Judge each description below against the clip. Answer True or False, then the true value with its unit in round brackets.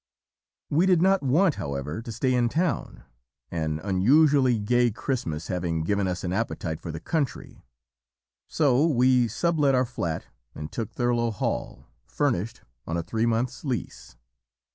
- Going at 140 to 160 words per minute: True (150 wpm)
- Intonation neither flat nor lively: False (7.3 semitones)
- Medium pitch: False (120 Hz)